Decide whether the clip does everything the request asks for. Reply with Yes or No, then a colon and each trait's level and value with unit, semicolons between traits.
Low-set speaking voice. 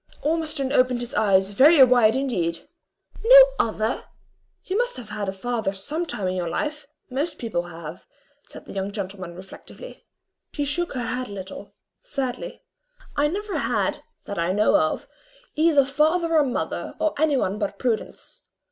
No: very high, 250 Hz